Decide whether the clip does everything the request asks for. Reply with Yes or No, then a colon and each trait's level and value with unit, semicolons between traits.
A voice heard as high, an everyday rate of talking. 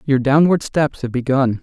No: low, 135 Hz; average, 185 wpm